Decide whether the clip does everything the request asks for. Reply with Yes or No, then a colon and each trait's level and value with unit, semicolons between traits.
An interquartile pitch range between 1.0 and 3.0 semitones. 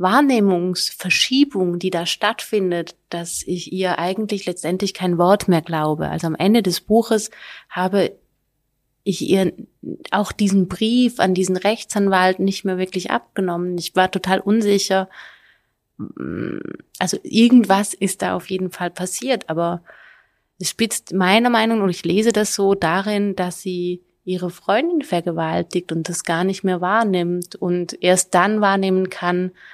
Yes: narrow, 2.5 semitones